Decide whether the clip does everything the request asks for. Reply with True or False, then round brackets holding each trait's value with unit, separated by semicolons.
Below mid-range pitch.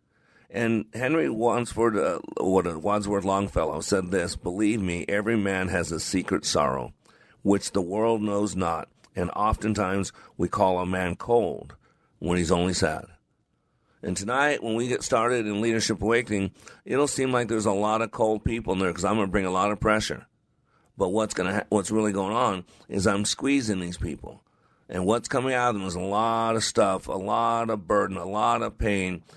True (105 Hz)